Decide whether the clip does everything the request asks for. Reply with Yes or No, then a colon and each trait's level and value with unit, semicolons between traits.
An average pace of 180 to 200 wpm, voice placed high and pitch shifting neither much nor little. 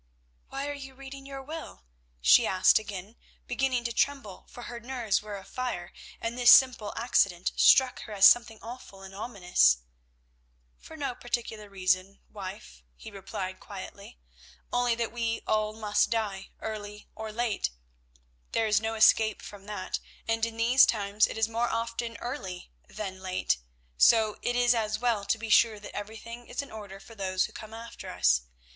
No: average, 170 wpm; high, 220 Hz; average, 3.3 semitones